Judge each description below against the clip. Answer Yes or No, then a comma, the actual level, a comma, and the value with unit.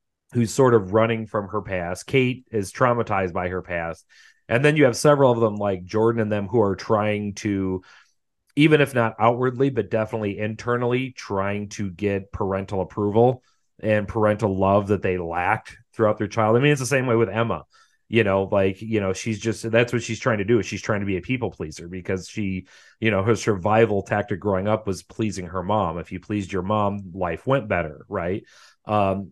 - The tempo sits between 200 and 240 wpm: Yes, fast, 205 wpm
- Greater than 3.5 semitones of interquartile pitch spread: No, average, 3.0 semitones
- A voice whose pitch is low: Yes, low, 105 Hz